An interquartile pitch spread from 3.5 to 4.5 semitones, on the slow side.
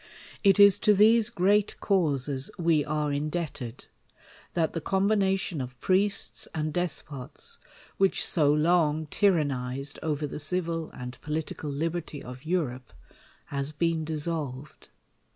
Yes: average, 4.0 semitones; slow, 120 wpm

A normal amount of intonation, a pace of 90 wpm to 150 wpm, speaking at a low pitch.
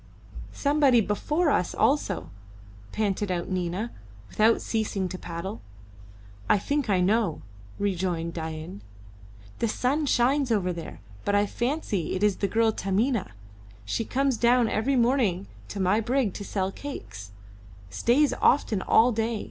No: average, 4.8 semitones; average, 140 wpm; high, 210 Hz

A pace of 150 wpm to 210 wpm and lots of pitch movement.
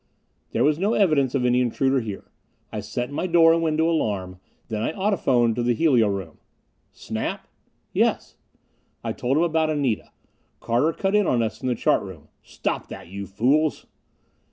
Yes: average, 175 wpm; wide, 6.4 semitones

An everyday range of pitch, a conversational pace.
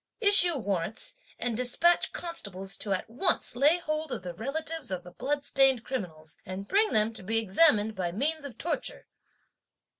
No: wide, 8.0 semitones; average, 160 wpm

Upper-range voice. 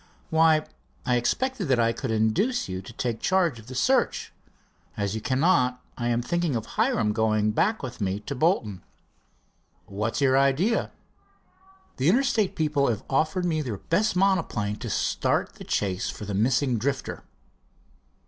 No: low, 130 Hz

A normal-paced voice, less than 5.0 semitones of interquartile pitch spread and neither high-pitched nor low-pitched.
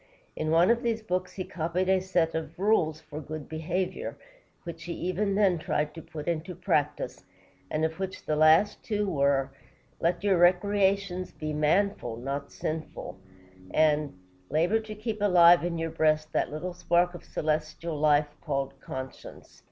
Yes: average, 160 wpm; average, 3.4 semitones; medium, 165 Hz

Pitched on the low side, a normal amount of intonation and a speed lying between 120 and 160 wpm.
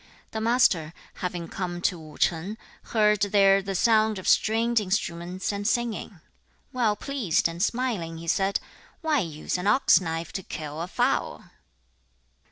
No: high, 195 Hz; average, 4.4 semitones; average, 155 wpm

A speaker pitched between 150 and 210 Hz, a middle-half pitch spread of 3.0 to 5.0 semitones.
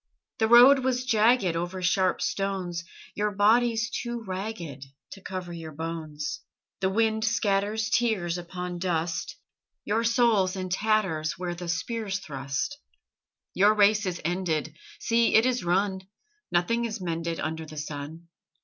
Yes: high, 190 Hz; average, 4.5 semitones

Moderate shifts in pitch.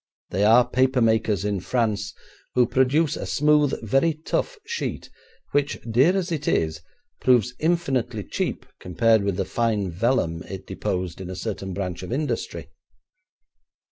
No: wide, 6.1 semitones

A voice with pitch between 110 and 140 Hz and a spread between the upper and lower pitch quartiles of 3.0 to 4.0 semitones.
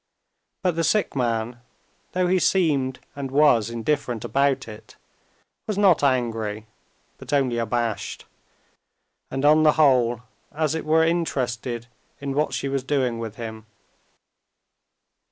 No: low, 135 Hz; average, 4.5 semitones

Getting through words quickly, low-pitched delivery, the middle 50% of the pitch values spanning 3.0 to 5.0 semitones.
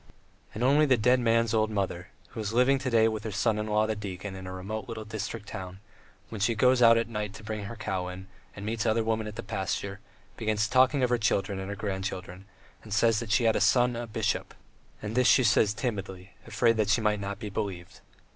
No: fast, 235 wpm; low, 110 Hz; narrow, 2.5 semitones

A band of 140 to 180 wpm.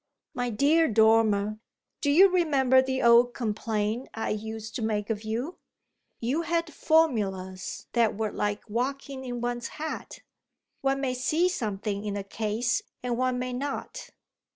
Yes: average, 150 wpm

